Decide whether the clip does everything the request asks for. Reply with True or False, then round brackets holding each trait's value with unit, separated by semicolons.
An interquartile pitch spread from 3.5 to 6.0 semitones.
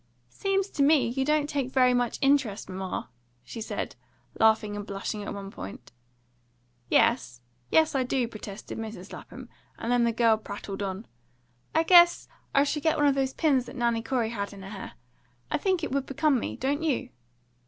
True (5.5 semitones)